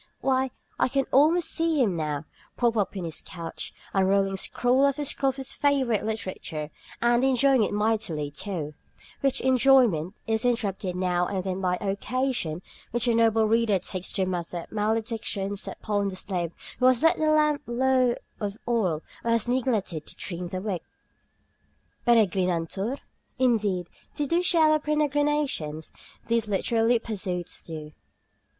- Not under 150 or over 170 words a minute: Yes, average, 155 wpm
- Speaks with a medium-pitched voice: No, high, 220 Hz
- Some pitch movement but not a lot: No, wide, 5.8 semitones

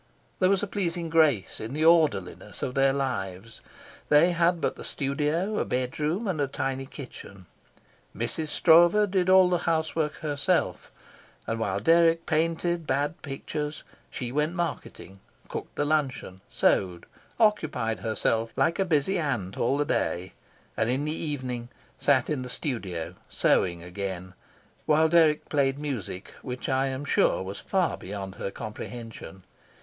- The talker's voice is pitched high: No, medium, 140 Hz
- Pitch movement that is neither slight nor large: No, wide, 6.3 semitones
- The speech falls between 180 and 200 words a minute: No, average, 150 wpm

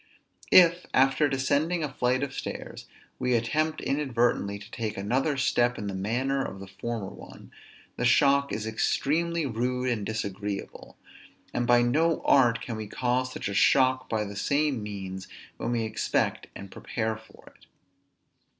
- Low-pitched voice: Yes, low, 120 Hz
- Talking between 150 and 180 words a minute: Yes, average, 160 wpm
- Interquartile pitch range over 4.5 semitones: No, average, 4.1 semitones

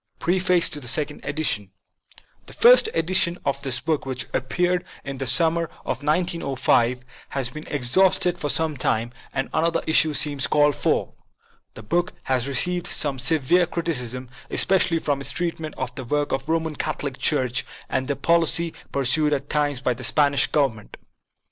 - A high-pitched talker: No, medium, 145 Hz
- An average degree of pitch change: Yes, average, 4.1 semitones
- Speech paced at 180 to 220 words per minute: No, average, 165 wpm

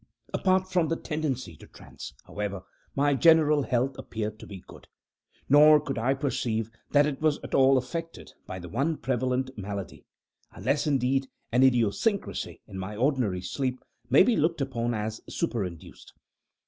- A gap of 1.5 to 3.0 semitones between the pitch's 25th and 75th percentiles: No, average, 5.2 semitones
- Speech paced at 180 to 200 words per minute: No, average, 155 wpm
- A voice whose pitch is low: Yes, low, 130 Hz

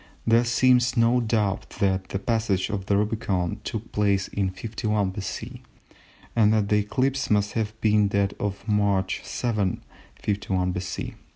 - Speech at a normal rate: Yes, average, 150 wpm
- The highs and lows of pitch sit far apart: No, narrow, 2.4 semitones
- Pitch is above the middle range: No, low, 105 Hz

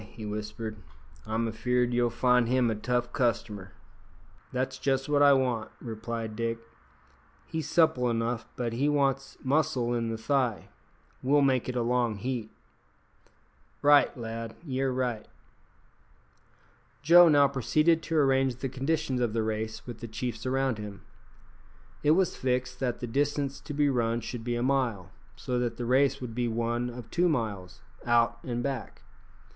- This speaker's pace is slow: No, average, 160 wpm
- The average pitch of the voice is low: Yes, low, 125 Hz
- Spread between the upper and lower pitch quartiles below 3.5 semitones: Yes, average, 2.8 semitones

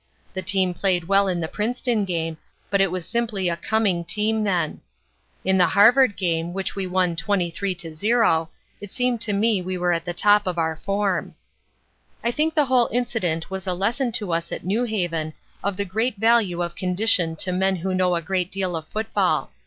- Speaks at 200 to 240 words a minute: Yes, fast, 205 wpm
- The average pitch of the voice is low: No, high, 190 Hz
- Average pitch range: Yes, average, 3.6 semitones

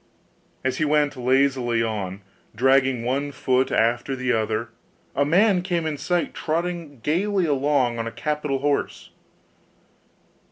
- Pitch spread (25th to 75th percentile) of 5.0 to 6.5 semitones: No, average, 3.9 semitones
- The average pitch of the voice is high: No, low, 135 Hz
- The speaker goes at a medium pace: No, slow, 125 wpm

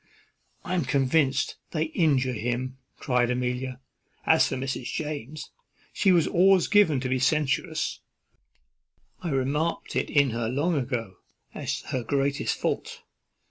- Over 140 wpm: No, slow, 135 wpm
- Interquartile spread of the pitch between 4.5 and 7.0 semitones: No, average, 3.6 semitones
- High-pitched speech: No, low, 135 Hz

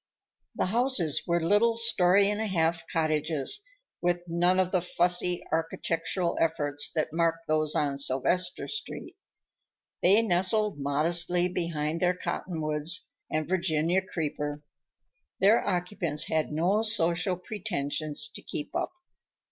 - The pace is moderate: No, slow, 125 wpm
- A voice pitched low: No, medium, 170 Hz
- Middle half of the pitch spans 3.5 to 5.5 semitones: No, average, 3.0 semitones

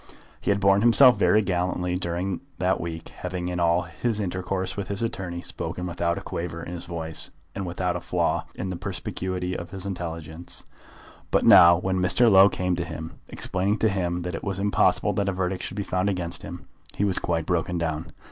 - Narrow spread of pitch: Yes, narrow, 2.1 semitones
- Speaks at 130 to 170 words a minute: No, fast, 205 wpm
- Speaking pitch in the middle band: No, very low, 90 Hz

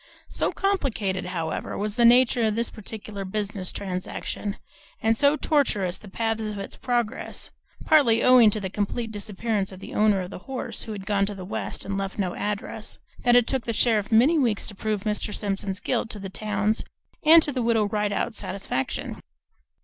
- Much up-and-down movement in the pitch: No, average, 2.9 semitones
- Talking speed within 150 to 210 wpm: Yes, average, 190 wpm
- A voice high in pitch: Yes, high, 210 Hz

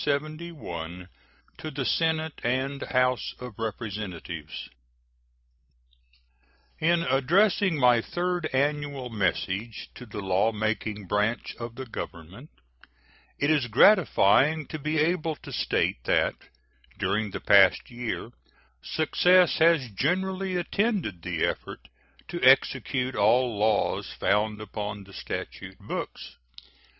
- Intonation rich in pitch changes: Yes, wide, 7.0 semitones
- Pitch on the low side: Yes, low, 125 Hz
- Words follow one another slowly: Yes, slow, 110 wpm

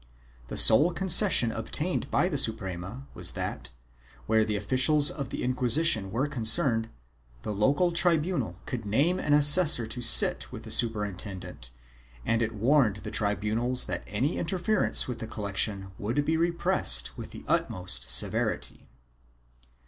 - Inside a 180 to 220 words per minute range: No, average, 140 wpm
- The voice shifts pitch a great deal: Yes, wide, 6.0 semitones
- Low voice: Yes, low, 120 Hz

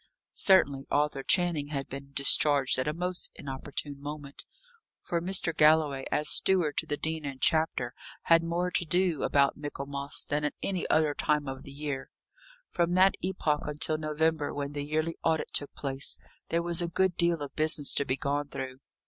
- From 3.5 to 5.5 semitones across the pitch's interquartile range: No, average, 3.0 semitones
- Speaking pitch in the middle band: Yes, medium, 150 Hz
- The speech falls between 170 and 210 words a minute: Yes, average, 180 wpm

